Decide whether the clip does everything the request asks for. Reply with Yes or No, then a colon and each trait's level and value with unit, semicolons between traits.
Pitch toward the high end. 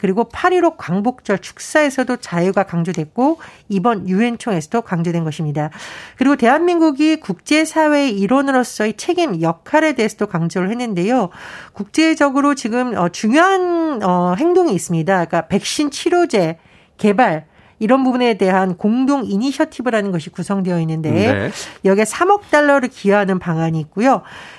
Yes: high, 220 Hz